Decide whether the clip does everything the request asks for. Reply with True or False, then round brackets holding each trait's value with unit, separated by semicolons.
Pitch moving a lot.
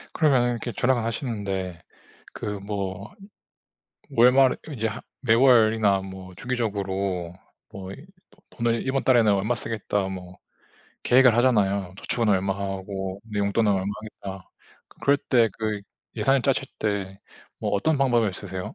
False (3.8 semitones)